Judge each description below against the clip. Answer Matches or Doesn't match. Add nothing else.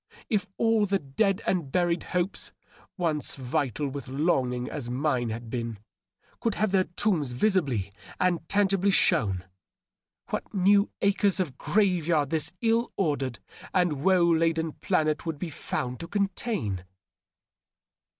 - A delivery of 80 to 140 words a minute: Matches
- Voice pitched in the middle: Matches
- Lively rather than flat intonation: Matches